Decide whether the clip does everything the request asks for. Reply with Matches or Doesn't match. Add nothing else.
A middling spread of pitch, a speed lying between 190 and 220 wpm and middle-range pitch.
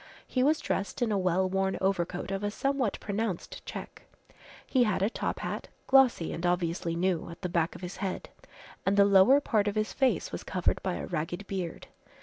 Doesn't match